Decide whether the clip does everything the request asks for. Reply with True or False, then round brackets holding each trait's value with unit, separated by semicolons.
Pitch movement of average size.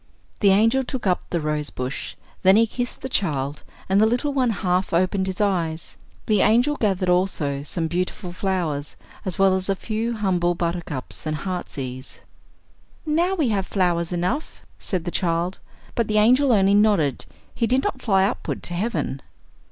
True (4.3 semitones)